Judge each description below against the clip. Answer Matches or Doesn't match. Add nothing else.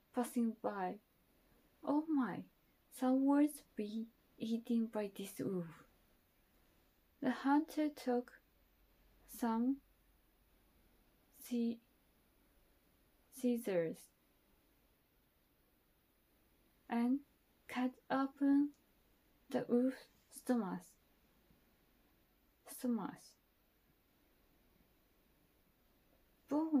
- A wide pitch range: Doesn't match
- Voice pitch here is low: Doesn't match